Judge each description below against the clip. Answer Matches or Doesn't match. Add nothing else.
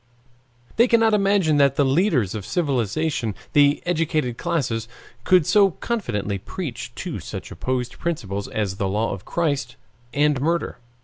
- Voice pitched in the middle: Matches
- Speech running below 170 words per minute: Matches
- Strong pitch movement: Matches